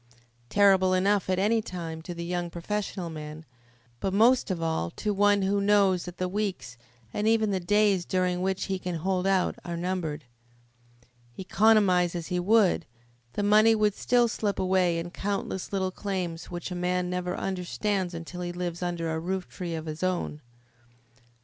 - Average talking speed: Yes, average, 175 wpm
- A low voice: No, medium, 185 Hz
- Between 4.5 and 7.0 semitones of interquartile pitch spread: No, narrow, 2.5 semitones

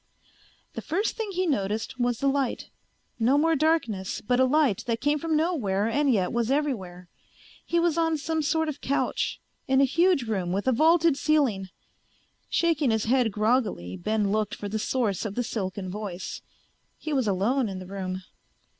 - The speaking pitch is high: Yes, high, 245 Hz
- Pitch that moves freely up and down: Yes, wide, 6.8 semitones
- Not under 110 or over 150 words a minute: No, average, 180 wpm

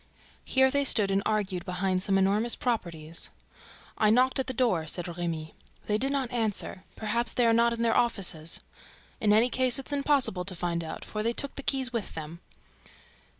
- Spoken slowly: No, average, 190 wpm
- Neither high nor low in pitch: No, high, 215 Hz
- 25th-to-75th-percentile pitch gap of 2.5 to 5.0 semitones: No, wide, 5.5 semitones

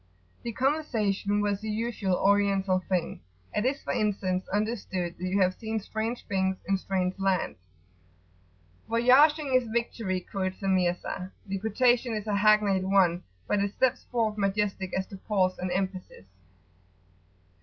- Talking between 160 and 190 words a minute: No, average, 145 wpm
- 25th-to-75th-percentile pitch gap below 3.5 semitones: Yes, average, 2.8 semitones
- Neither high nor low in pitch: No, high, 200 Hz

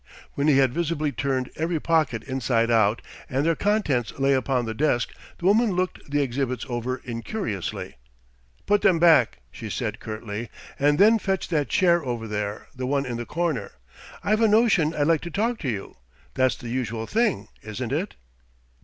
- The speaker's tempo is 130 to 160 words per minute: No, average, 180 wpm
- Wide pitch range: Yes, wide, 6.4 semitones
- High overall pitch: No, medium, 140 Hz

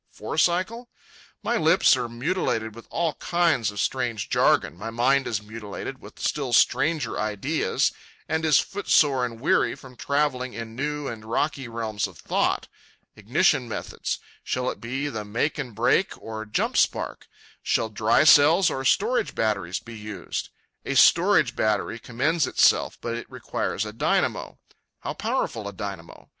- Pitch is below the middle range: Yes, low, 120 Hz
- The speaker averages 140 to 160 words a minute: Yes, average, 150 wpm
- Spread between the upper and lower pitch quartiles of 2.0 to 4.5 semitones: No, average, 5.2 semitones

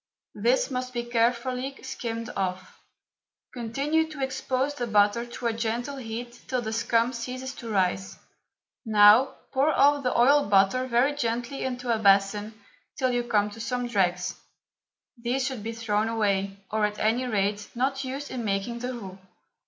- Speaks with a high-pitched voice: Yes, high, 235 Hz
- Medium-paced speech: Yes, average, 160 wpm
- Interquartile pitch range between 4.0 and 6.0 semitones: No, average, 3.4 semitones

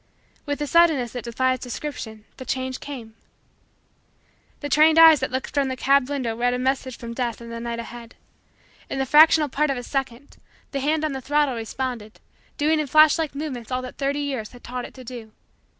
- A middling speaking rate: No, fast, 210 wpm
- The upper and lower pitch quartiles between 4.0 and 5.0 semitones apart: No, average, 3.1 semitones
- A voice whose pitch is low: No, very high, 260 Hz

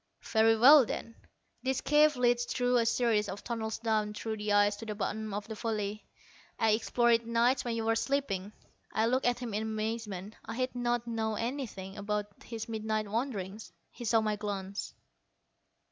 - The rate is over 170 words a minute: Yes, average, 185 wpm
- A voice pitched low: No, high, 225 Hz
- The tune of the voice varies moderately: No, narrow, 2.3 semitones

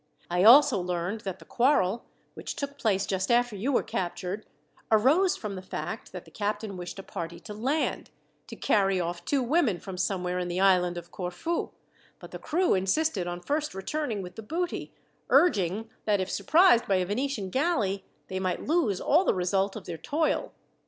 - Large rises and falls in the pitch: Yes, wide, 6.7 semitones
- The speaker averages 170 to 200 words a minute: Yes, average, 185 wpm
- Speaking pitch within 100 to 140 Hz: No, high, 200 Hz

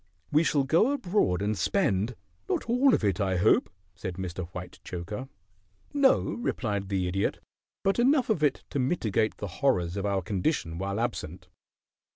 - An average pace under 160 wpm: No, average, 165 wpm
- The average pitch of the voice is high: No, low, 105 Hz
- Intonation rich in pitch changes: Yes, wide, 9.0 semitones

